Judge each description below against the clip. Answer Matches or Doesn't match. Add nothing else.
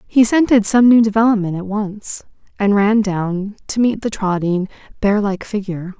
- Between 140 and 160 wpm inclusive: Doesn't match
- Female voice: Matches